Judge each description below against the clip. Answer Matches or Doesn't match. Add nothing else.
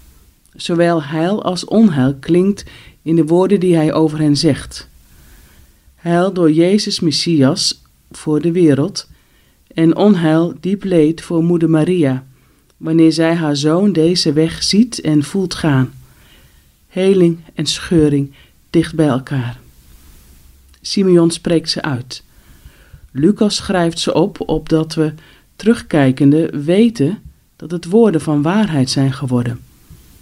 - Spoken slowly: Matches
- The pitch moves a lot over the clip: Doesn't match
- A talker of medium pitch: Matches